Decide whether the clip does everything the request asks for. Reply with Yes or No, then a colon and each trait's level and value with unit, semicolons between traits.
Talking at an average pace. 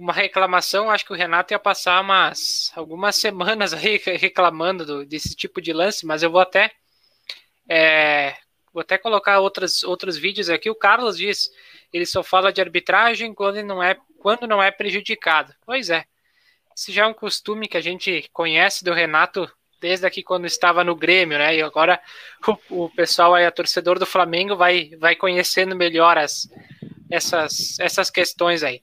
Yes: average, 175 wpm